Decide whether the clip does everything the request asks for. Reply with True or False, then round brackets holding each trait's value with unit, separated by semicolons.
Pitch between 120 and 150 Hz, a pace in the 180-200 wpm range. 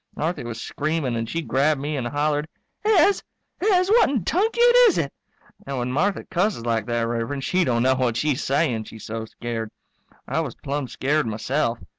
True (140 Hz; 185 wpm)